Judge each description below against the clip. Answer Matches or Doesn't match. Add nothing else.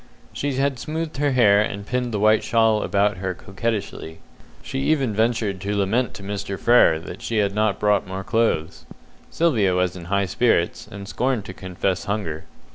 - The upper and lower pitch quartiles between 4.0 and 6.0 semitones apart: Doesn't match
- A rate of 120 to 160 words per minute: Doesn't match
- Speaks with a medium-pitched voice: Doesn't match